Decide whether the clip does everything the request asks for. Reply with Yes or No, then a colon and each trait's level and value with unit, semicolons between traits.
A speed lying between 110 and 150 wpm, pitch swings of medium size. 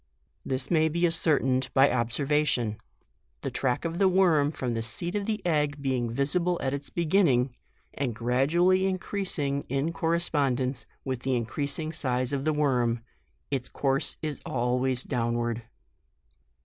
Yes: average, 145 wpm; average, 4.6 semitones